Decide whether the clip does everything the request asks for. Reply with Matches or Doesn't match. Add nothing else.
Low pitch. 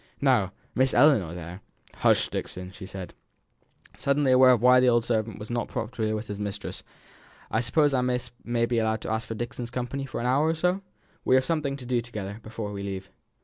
Matches